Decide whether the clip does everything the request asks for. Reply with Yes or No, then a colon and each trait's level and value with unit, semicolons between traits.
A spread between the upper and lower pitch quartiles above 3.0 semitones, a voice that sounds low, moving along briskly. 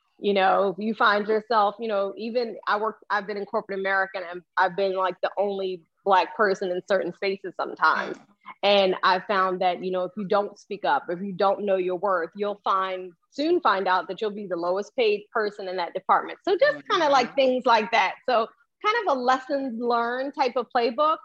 No: average, 3.9 semitones; high, 205 Hz; fast, 215 wpm